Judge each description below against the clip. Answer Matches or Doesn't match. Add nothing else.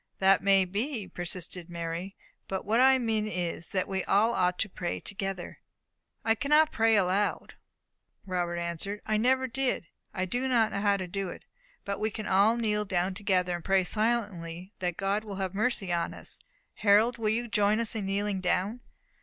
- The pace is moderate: Matches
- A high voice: Matches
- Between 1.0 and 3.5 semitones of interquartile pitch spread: Matches